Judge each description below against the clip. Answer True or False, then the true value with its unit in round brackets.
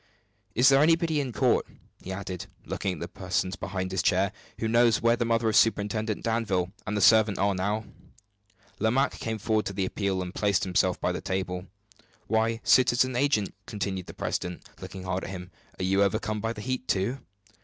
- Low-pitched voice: True (105 Hz)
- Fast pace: False (190 wpm)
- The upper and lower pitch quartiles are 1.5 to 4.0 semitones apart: True (3.5 semitones)